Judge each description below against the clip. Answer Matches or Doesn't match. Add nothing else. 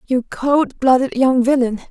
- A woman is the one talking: Matches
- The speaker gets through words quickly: Doesn't match